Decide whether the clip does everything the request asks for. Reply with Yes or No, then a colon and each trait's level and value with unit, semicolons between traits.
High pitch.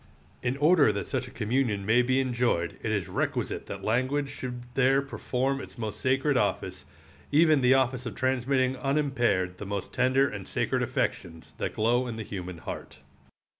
No: low, 125 Hz